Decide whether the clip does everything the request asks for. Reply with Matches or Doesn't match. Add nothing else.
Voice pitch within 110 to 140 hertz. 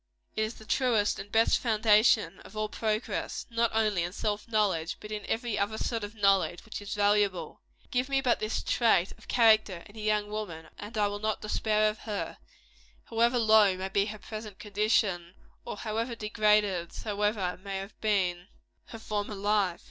Doesn't match